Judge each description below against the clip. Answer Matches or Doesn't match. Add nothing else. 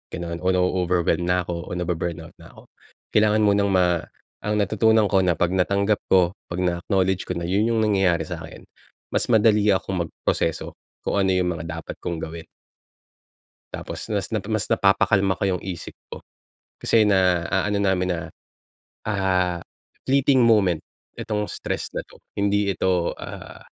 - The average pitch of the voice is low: Matches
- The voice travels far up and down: Doesn't match